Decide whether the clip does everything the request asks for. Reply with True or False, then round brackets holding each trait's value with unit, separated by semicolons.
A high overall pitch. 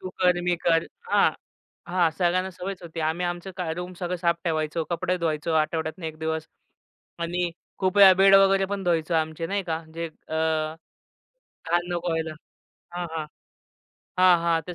False (175 Hz)